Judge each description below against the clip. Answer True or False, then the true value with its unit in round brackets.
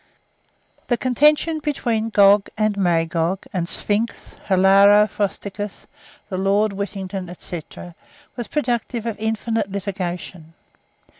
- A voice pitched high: True (205 Hz)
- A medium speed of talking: False (105 wpm)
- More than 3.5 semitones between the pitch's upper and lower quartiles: False (3.0 semitones)